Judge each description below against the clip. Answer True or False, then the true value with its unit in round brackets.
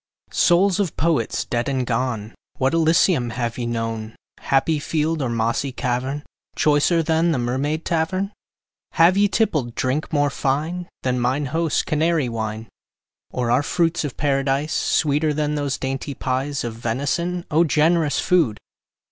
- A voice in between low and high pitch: True (145 Hz)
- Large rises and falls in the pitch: False (4.5 semitones)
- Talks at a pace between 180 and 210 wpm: False (150 wpm)